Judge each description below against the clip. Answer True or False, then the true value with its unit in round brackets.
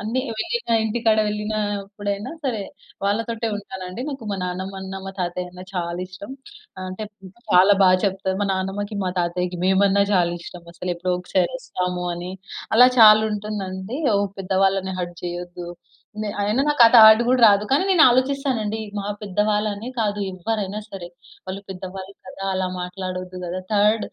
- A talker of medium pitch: False (200 Hz)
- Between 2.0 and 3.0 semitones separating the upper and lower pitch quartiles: True (2.7 semitones)